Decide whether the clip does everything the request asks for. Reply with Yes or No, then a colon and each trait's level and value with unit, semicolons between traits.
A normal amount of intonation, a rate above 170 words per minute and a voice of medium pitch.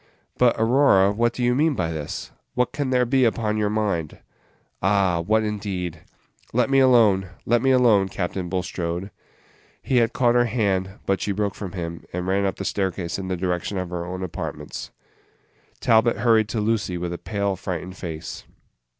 No: average, 4.3 semitones; average, 180 wpm; low, 100 Hz